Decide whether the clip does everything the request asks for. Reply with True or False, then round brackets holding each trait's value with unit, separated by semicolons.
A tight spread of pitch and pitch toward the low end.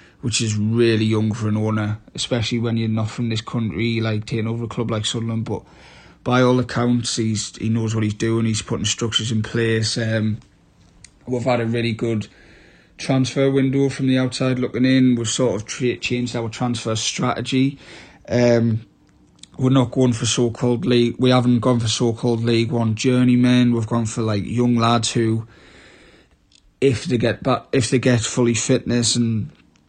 True (1.9 semitones; 115 Hz)